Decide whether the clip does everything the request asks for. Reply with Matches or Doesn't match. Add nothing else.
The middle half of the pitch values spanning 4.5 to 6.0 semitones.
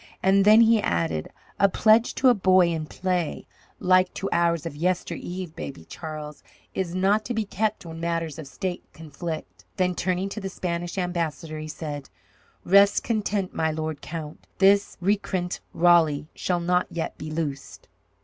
Doesn't match